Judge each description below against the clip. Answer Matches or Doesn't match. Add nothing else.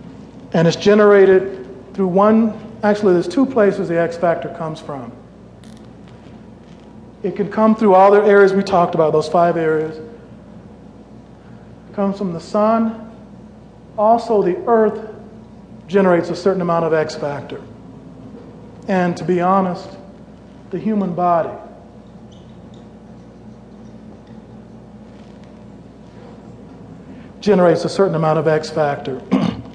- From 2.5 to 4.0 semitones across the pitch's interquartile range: Matches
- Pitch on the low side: Doesn't match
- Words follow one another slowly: Matches